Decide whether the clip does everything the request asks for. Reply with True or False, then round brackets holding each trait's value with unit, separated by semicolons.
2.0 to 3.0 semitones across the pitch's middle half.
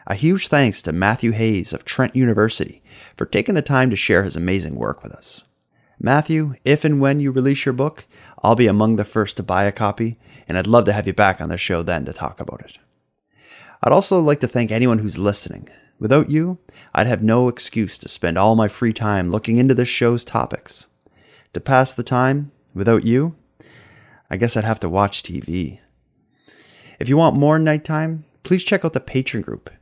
False (5.3 semitones)